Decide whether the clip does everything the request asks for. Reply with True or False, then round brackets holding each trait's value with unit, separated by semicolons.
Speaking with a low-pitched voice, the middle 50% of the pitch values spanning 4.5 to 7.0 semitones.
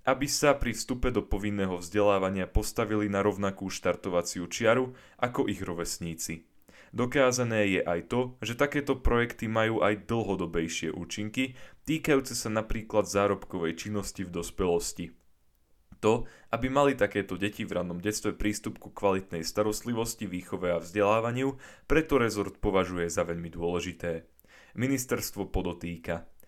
True (105 Hz; 5.0 semitones)